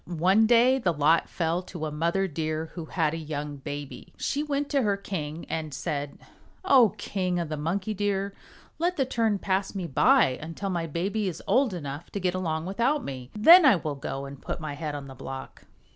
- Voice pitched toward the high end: No, medium, 175 Hz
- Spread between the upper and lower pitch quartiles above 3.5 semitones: Yes, average, 5.2 semitones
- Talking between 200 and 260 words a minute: Yes, fast, 205 wpm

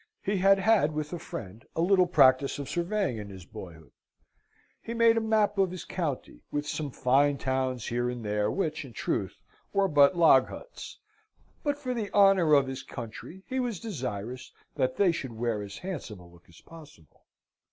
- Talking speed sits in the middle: Yes, average, 185 wpm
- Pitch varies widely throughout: Yes, wide, 8.1 semitones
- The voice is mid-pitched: Yes, medium, 145 Hz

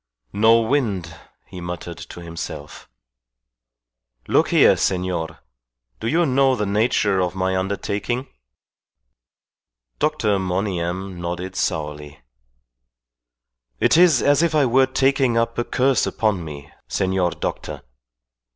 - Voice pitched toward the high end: No, low, 100 Hz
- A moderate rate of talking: No, slow, 115 wpm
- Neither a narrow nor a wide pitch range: No, wide, 6.2 semitones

